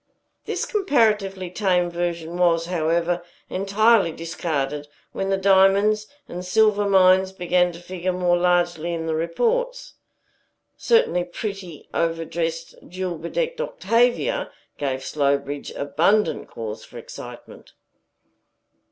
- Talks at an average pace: No, slow, 110 wpm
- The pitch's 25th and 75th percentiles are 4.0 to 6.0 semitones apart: No, average, 3.2 semitones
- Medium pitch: Yes, medium, 180 Hz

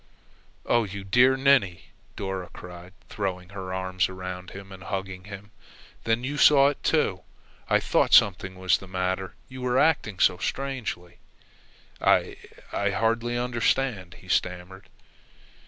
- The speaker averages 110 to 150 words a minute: Yes, average, 140 wpm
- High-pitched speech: No, very low, 95 Hz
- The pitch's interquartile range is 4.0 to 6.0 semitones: Yes, average, 4.5 semitones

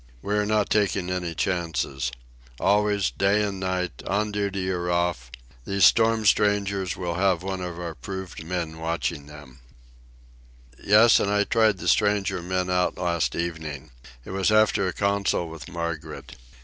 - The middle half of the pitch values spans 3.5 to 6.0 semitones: No, average, 3.1 semitones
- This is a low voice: Yes, very low, 95 Hz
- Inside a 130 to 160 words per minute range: Yes, average, 155 wpm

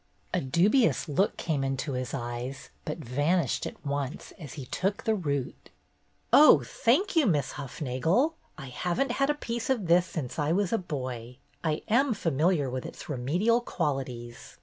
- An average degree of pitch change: No, wide, 7.3 semitones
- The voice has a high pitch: No, medium, 155 Hz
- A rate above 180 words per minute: No, average, 170 wpm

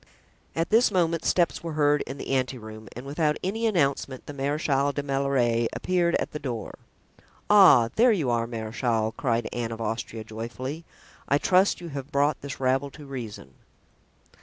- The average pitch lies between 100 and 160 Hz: Yes, medium, 140 Hz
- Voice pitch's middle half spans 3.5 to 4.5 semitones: No, average, 5.2 semitones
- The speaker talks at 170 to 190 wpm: Yes, average, 175 wpm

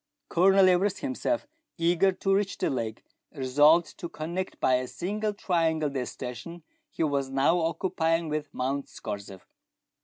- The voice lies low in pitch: No, medium, 165 Hz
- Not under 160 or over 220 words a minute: No, average, 145 wpm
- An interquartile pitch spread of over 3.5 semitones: Yes, wide, 5.4 semitones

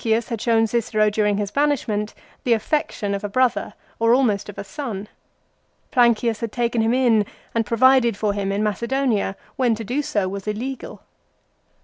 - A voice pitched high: Yes, high, 225 Hz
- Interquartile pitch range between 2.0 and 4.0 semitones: Yes, average, 2.8 semitones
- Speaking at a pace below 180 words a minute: Yes, average, 170 wpm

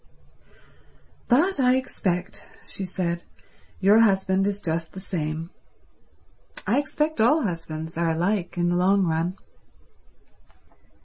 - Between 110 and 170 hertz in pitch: No, high, 190 Hz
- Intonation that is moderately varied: Yes, average, 4.4 semitones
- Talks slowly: Yes, slow, 115 wpm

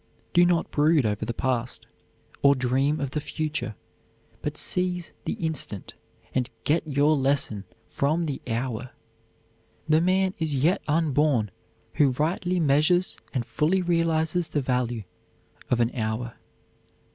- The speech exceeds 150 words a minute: No, slow, 135 wpm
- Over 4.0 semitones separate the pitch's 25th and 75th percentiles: Yes, average, 4.5 semitones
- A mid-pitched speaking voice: Yes, medium, 145 Hz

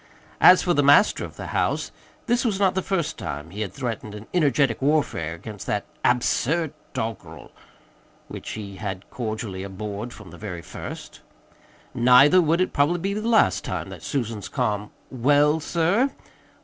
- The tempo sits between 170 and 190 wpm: No, average, 160 wpm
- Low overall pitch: Yes, low, 125 Hz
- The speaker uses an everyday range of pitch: No, wide, 7.8 semitones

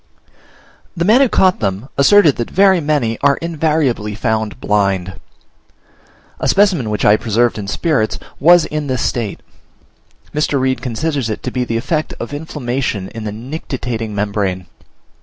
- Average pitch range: No, wide, 6.1 semitones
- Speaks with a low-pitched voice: Yes, low, 125 Hz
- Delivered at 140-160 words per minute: Yes, average, 150 wpm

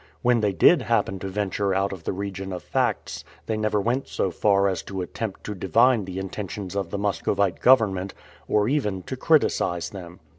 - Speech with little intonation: Yes, narrow, 2.3 semitones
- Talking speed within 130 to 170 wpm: No, average, 190 wpm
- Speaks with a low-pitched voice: Yes, low, 100 Hz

